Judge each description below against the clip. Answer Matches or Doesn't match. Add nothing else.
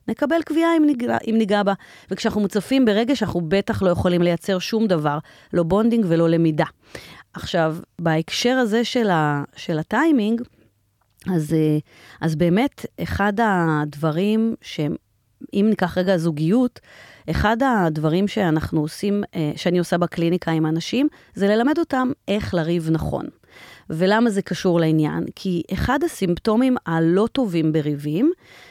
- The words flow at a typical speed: Matches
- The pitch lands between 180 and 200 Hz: Matches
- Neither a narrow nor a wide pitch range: Doesn't match